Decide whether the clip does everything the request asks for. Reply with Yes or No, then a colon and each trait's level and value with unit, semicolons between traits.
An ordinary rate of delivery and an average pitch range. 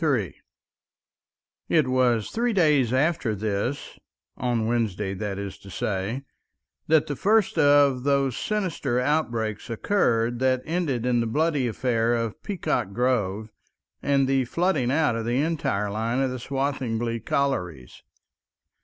No: slow, 130 wpm; average, 4.2 semitones